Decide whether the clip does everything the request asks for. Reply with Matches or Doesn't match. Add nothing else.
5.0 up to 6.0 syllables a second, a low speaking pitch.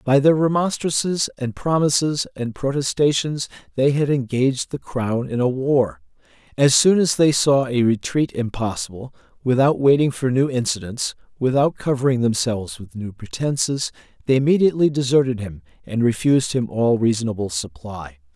Matches